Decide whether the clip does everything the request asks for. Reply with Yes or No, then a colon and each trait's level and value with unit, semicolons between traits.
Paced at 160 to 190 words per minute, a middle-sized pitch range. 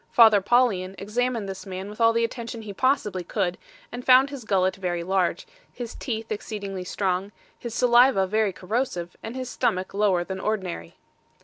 Yes: average, 170 wpm; average, 3.9 semitones